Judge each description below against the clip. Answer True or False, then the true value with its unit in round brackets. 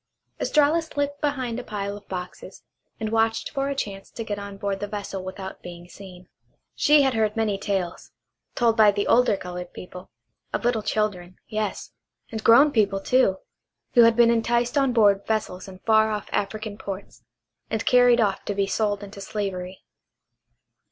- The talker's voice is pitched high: True (210 Hz)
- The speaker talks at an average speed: True (170 wpm)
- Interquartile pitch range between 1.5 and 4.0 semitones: True (3.1 semitones)